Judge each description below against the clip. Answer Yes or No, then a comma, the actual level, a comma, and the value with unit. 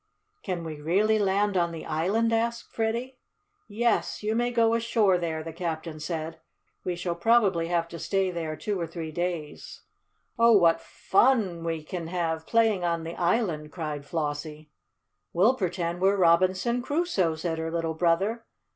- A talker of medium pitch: Yes, medium, 175 Hz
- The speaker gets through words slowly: No, average, 160 wpm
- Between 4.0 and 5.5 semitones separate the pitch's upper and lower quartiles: Yes, average, 4.7 semitones